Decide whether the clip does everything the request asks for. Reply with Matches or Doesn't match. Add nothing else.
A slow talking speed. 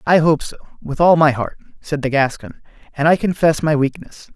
Doesn't match